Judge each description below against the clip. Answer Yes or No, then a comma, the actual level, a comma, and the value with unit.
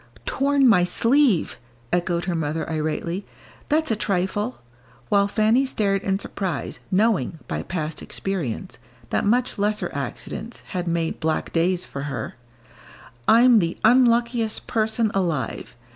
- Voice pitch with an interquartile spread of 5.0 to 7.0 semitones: Yes, average, 5.3 semitones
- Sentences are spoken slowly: Yes, slow, 130 wpm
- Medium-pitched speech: No, high, 195 Hz